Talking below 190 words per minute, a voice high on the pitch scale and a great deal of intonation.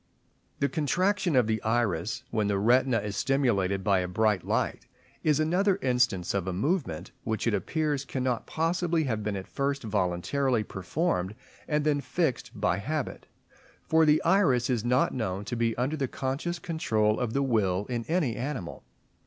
No: average, 170 wpm; low, 125 Hz; wide, 6.2 semitones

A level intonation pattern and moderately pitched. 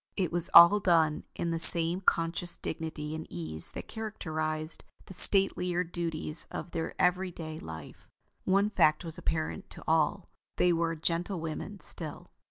Yes: narrow, 2.2 semitones; medium, 165 Hz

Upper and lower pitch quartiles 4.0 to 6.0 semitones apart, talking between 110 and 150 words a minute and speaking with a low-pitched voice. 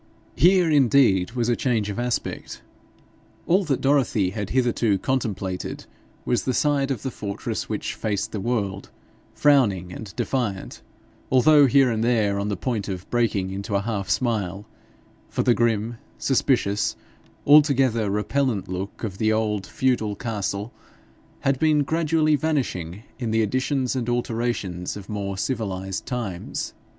Yes: average, 4.8 semitones; average, 140 wpm; low, 115 Hz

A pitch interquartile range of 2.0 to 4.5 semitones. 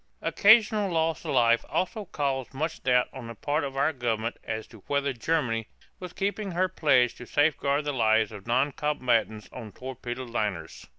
No: average, 5.3 semitones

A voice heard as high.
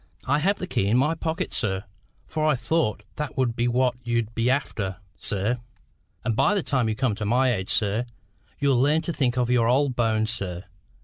No: low, 120 Hz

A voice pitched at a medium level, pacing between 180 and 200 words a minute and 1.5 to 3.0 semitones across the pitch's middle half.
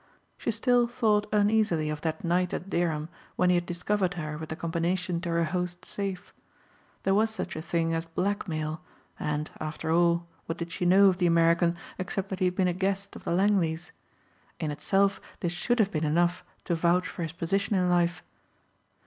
Yes: medium, 175 Hz; average, 195 wpm; average, 2.7 semitones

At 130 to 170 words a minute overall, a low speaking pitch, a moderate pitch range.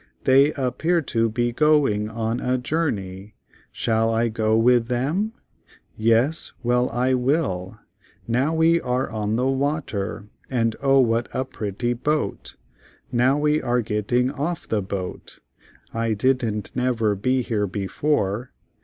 Yes: average, 150 wpm; low, 120 Hz; average, 3.5 semitones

